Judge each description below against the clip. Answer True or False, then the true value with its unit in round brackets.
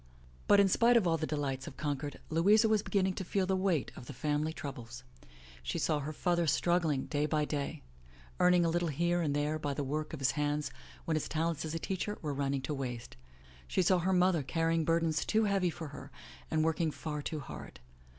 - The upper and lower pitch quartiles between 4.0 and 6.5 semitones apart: False (3.3 semitones)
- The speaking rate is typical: False (220 wpm)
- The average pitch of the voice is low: False (155 Hz)